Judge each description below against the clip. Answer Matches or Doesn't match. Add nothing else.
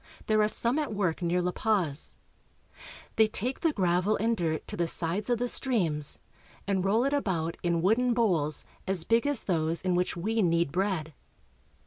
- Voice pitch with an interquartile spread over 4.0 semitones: Matches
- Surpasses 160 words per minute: Matches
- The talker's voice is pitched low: Doesn't match